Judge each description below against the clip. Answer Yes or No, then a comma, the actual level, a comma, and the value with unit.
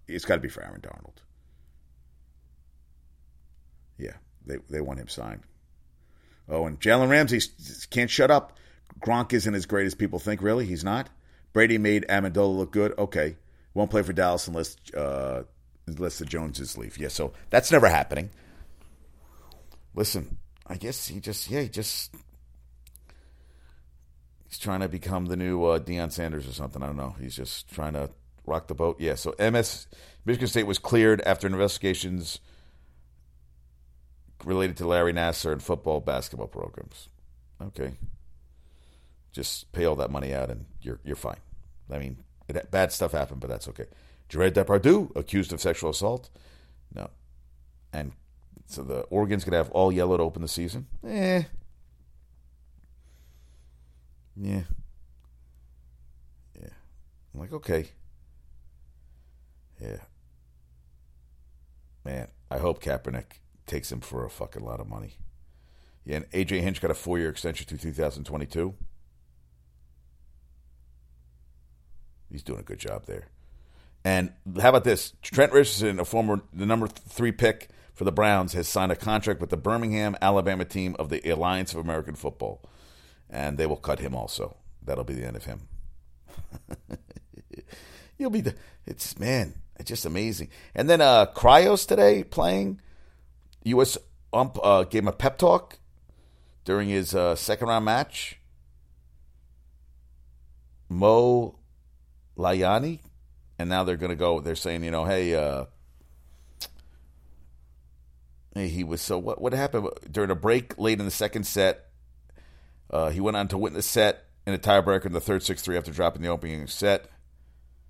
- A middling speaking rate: Yes, average, 150 wpm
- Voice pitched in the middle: No, very low, 70 Hz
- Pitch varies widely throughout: Yes, wide, 7.0 semitones